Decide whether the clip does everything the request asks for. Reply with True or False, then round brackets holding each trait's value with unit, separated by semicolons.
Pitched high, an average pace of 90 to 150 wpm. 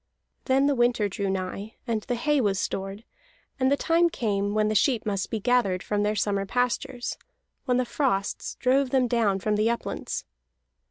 False (225 Hz; 180 wpm)